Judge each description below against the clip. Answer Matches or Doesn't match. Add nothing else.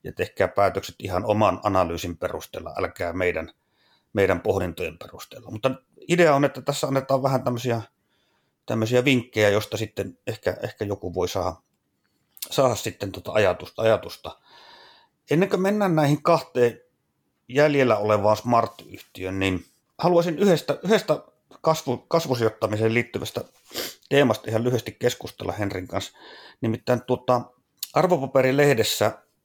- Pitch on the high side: Doesn't match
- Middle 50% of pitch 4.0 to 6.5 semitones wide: Matches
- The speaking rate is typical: Matches